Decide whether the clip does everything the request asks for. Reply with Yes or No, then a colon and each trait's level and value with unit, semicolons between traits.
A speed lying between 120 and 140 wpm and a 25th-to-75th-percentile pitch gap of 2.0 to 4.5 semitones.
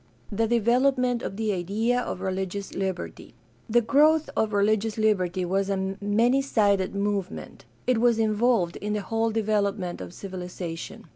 No: average, 150 wpm; average, 3.1 semitones